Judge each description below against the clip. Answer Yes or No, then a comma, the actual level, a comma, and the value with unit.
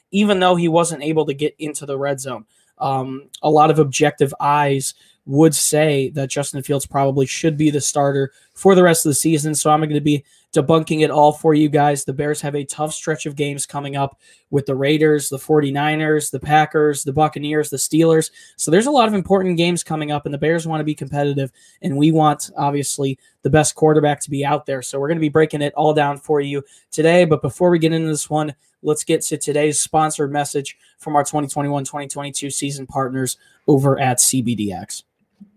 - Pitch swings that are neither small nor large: No, narrow, 1.7 semitones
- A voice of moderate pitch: Yes, medium, 150 Hz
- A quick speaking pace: Yes, fast, 215 wpm